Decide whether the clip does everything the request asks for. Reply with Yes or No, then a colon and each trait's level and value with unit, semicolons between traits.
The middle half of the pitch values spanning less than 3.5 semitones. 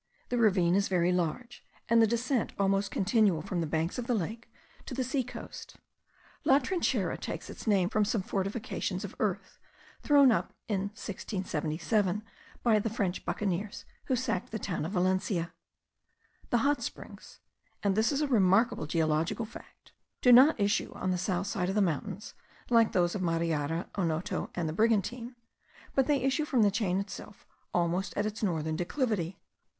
No: average, 4.6 semitones